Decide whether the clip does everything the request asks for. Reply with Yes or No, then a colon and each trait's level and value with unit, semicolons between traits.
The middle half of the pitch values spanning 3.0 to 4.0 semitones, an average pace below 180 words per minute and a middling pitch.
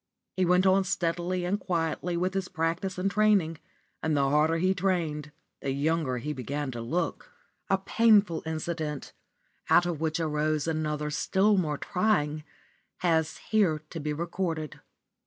Yes: average, 3.5 semitones; average, 150 wpm; medium, 165 Hz